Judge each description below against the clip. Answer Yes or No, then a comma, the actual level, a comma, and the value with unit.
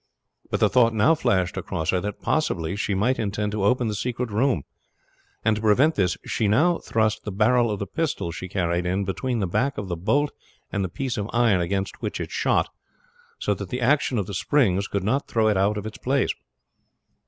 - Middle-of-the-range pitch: No, low, 105 Hz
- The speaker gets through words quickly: Yes, fast, 215 wpm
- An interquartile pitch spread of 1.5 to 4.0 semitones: No, average, 4.4 semitones